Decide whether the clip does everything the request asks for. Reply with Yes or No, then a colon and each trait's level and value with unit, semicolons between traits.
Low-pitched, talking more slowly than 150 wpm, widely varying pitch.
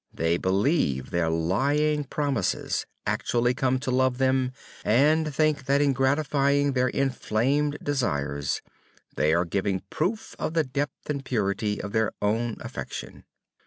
Yes: low, 130 Hz; average, 140 wpm; wide, 5.8 semitones